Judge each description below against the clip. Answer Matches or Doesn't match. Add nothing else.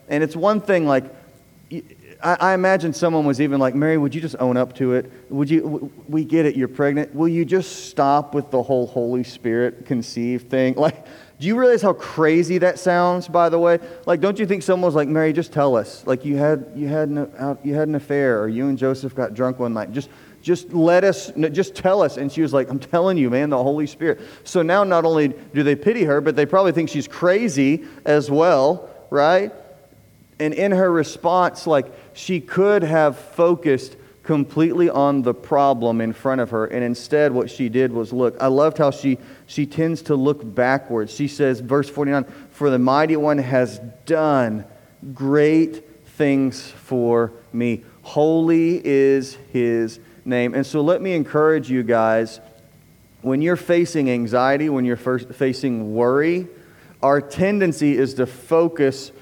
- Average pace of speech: Matches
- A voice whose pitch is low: Doesn't match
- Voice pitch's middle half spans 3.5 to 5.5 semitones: Matches